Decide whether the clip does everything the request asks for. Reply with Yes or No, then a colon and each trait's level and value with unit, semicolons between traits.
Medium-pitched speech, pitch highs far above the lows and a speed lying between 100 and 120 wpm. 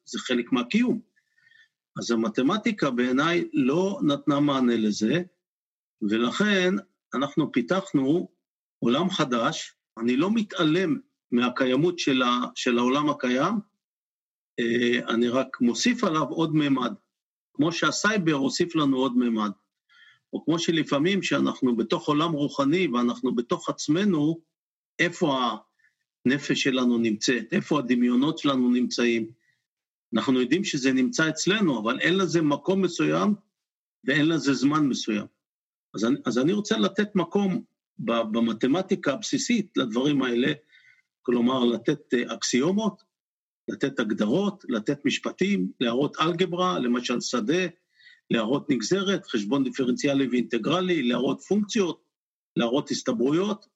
Yes: medium, 150 Hz; wide, 7.9 semitones; average, 110 wpm